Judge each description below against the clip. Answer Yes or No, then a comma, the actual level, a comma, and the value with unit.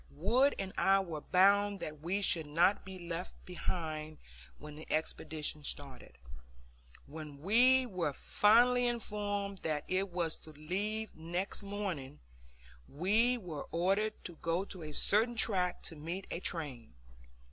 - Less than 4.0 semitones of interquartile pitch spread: No, average, 4.7 semitones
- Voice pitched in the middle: Yes, medium, 180 Hz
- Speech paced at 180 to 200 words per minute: No, average, 140 wpm